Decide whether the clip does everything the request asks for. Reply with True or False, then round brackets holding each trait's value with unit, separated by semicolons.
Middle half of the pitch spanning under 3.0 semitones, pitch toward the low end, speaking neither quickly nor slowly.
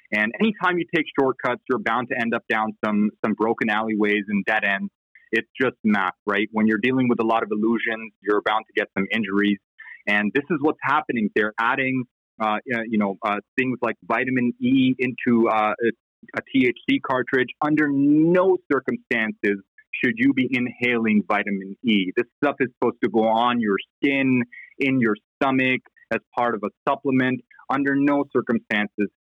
False (4.0 semitones; 120 Hz; 175 wpm)